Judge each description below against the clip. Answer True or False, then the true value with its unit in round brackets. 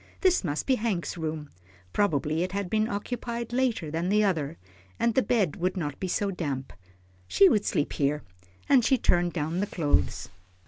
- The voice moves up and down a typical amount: False (5.7 semitones)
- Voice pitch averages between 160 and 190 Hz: True (185 Hz)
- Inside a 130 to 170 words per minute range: False (180 wpm)